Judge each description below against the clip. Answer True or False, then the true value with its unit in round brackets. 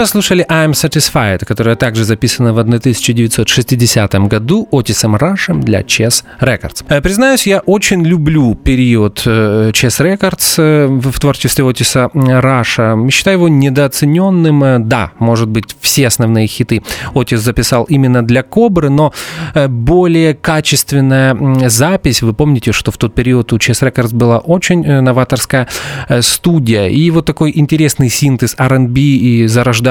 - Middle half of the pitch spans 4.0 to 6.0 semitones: True (4.5 semitones)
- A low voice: True (130 Hz)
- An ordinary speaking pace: True (130 wpm)